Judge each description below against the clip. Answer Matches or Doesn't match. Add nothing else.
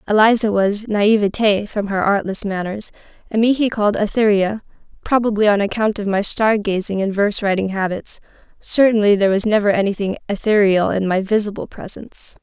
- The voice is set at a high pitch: Matches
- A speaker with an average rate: Matches